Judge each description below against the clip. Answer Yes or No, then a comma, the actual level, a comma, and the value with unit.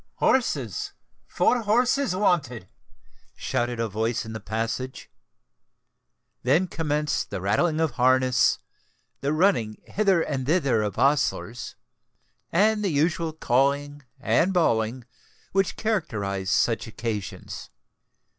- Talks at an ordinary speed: No, slow, 100 wpm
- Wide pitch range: Yes, wide, 7.2 semitones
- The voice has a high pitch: No, medium, 140 Hz